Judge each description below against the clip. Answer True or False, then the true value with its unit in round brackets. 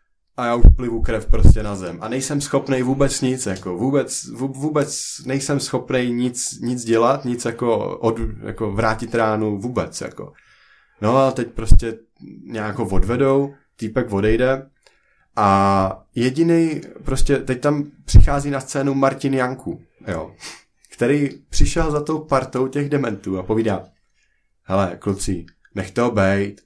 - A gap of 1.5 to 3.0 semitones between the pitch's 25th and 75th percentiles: False (4.5 semitones)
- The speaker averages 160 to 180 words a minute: False (140 wpm)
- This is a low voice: True (120 Hz)